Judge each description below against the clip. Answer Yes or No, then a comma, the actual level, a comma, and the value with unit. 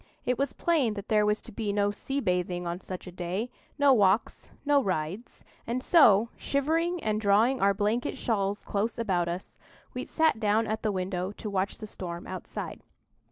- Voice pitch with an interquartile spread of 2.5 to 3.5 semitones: No, average, 4.1 semitones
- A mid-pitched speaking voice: No, high, 210 Hz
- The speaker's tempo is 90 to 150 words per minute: No, average, 185 wpm